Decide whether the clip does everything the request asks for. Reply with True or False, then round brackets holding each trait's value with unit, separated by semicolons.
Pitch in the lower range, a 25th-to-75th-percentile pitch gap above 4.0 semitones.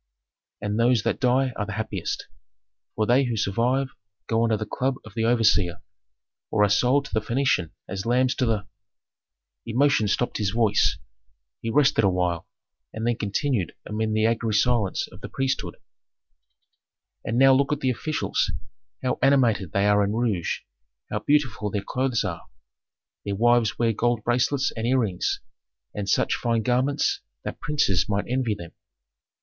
False (115 Hz; 3.6 semitones)